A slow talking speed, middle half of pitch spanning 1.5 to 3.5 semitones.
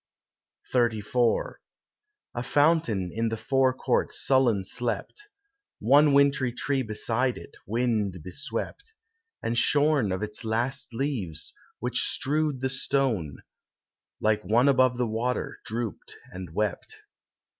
No: slow, 115 wpm; average, 3.9 semitones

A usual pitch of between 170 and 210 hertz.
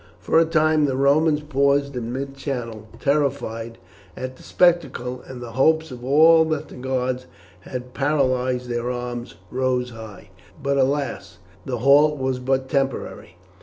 No: low, 130 Hz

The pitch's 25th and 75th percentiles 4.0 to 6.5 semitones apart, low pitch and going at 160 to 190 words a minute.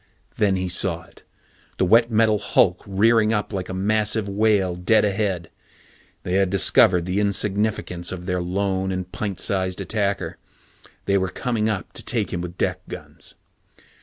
No: narrow, 2.5 semitones; very low, 95 Hz; average, 165 wpm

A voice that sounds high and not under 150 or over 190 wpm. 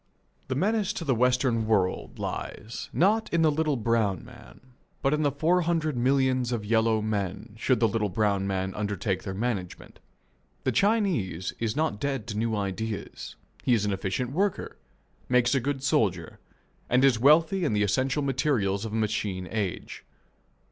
No: low, 115 Hz; average, 170 wpm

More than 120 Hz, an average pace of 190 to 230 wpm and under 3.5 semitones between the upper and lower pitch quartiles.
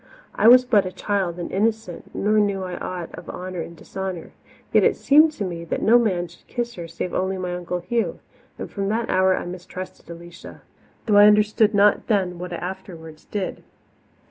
Yes: high, 190 Hz; average, 195 wpm; average, 3.0 semitones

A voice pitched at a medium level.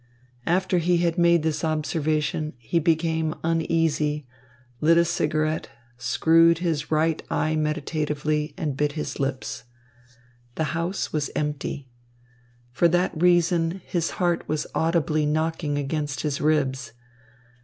Yes: medium, 155 Hz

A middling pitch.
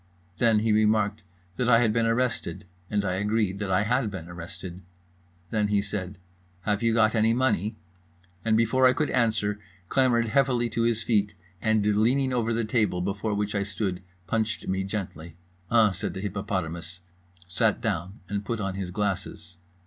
No: low, 105 Hz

